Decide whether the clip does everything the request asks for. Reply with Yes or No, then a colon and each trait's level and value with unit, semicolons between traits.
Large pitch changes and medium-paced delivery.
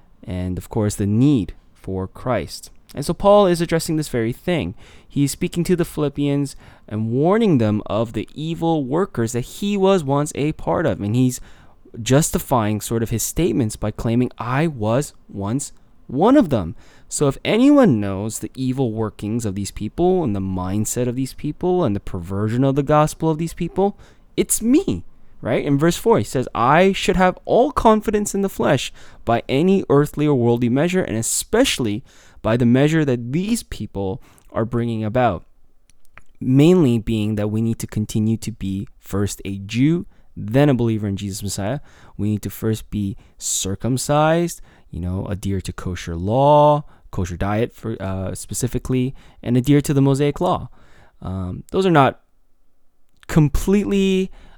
Yes: wide, 6.9 semitones; average, 170 wpm